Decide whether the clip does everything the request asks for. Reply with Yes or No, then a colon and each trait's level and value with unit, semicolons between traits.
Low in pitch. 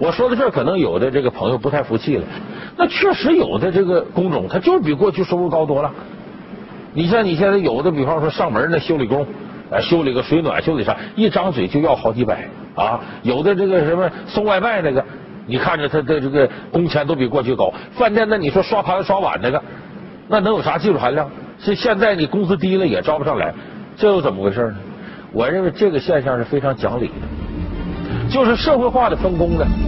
No: medium, 185 Hz